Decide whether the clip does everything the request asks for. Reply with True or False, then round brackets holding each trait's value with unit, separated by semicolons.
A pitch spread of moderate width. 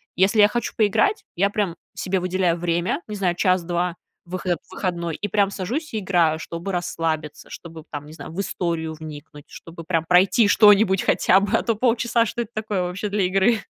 True (3.5 semitones)